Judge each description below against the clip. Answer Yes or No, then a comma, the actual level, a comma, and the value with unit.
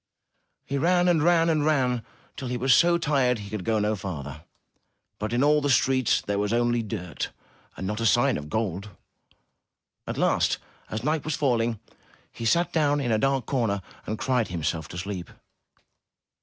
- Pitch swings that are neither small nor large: No, wide, 5.7 semitones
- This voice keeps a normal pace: Yes, average, 180 wpm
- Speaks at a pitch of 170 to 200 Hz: No, low, 120 Hz